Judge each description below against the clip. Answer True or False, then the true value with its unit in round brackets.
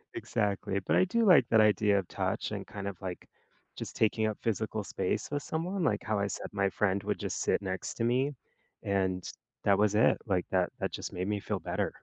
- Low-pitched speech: True (105 Hz)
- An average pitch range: True (3.0 semitones)